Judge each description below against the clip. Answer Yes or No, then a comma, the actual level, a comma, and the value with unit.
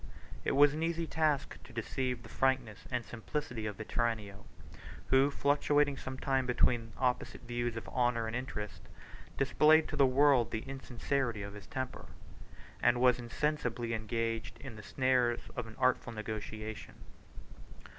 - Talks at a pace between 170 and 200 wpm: No, average, 150 wpm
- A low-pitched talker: Yes, low, 125 Hz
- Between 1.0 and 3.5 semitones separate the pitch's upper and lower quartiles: Yes, average, 3.1 semitones